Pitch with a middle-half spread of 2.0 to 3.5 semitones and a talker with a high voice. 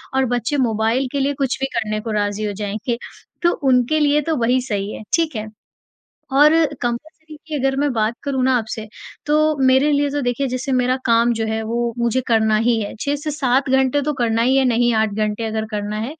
No: average, 4.0 semitones; high, 245 Hz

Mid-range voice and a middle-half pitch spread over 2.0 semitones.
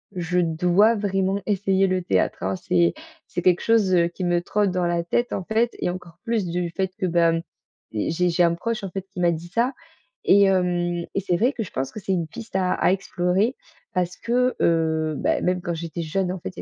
Yes: medium, 180 Hz; narrow, 2.4 semitones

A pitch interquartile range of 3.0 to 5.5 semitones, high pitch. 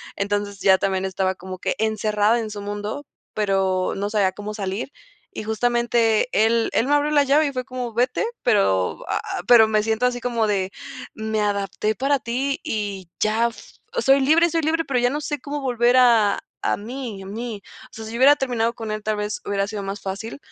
Yes: average, 3.6 semitones; high, 220 Hz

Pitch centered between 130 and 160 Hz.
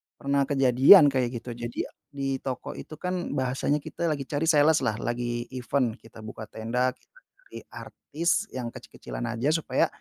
Yes: low, 135 Hz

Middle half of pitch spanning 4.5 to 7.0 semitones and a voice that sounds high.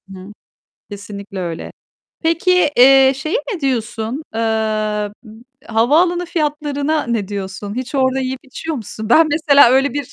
Yes: wide, 5.4 semitones; very high, 265 Hz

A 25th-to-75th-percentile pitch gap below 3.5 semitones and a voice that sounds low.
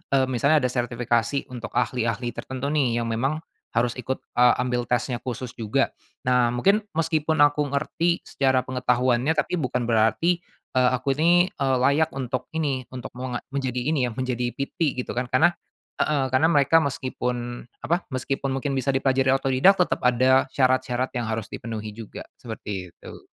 Yes: narrow, 2.5 semitones; low, 130 Hz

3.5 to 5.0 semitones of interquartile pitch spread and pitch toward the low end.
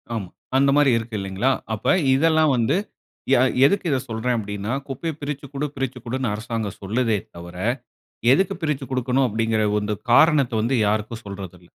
Yes: average, 4.4 semitones; low, 120 Hz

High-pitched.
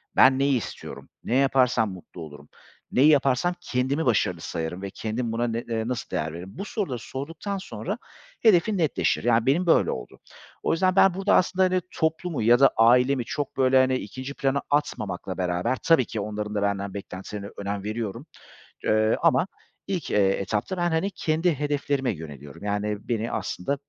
No: low, 125 Hz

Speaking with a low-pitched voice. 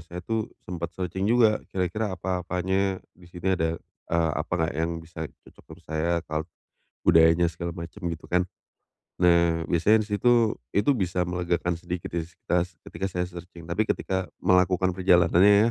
Yes: very low, 90 Hz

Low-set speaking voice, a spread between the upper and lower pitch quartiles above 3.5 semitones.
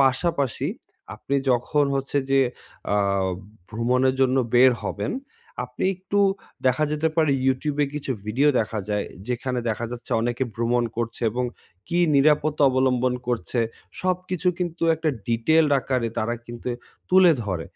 Yes: low, 130 Hz; average, 4.0 semitones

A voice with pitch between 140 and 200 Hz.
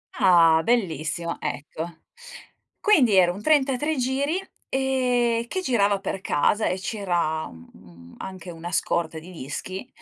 Yes: high, 190 Hz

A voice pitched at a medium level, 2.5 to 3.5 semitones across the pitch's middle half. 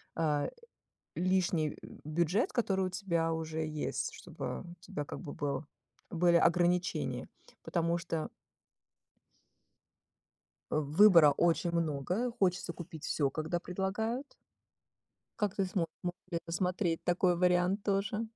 Yes: medium, 175 Hz; average, 2.8 semitones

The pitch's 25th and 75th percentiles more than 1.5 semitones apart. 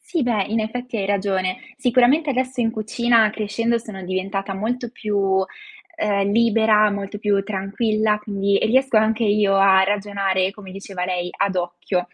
Yes: narrow, 2.6 semitones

